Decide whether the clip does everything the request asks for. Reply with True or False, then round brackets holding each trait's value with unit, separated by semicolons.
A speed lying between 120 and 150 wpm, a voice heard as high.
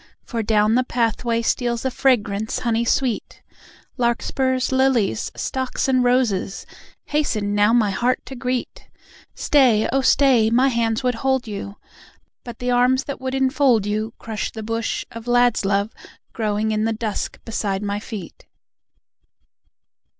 True (145 wpm; 235 Hz)